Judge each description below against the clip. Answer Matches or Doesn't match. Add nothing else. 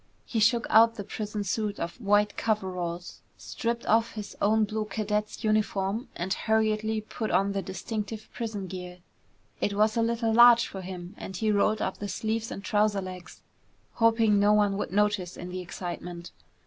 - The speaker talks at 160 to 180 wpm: Matches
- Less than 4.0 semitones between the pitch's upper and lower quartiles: Matches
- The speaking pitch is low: Doesn't match